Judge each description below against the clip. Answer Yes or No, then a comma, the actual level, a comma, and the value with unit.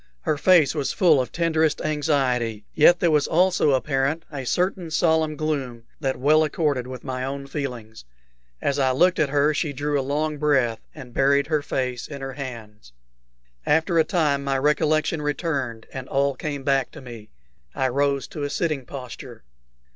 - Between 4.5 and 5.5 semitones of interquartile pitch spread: No, average, 2.9 semitones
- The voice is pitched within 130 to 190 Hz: Yes, medium, 140 Hz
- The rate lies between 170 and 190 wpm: Yes, average, 175 wpm